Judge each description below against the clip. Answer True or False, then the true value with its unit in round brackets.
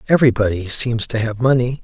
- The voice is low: True (120 Hz)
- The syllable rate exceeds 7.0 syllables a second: False (6.1 syllables/s)